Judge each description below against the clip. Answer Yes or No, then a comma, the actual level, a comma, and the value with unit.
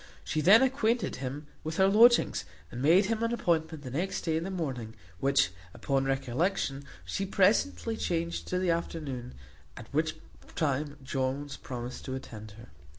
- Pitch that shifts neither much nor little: No, wide, 6.0 semitones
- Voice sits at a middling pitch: Yes, medium, 155 Hz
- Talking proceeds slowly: No, average, 160 wpm